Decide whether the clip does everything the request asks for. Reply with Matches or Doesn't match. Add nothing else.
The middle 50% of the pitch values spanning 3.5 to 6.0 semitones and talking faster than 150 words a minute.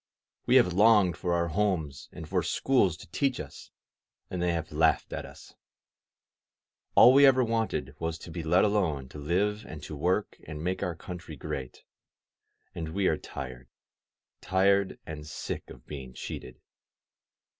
Matches